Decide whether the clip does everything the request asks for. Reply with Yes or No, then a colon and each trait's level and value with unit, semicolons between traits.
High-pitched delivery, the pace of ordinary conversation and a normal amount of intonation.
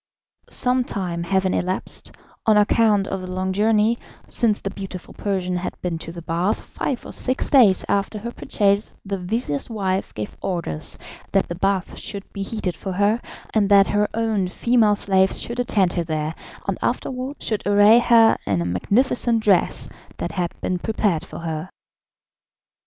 Yes: high, 195 Hz; average, 170 wpm; average, 3.4 semitones